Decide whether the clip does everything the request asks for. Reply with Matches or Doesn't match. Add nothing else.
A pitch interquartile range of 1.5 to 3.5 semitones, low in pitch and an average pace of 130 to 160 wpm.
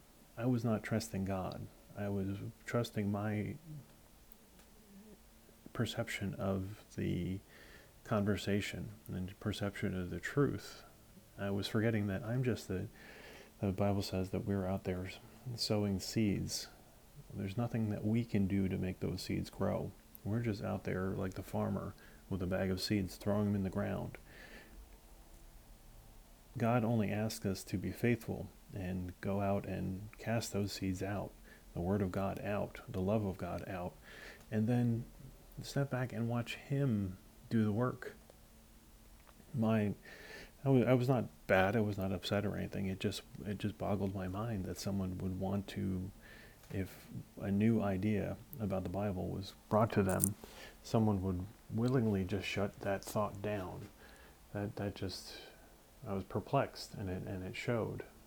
Matches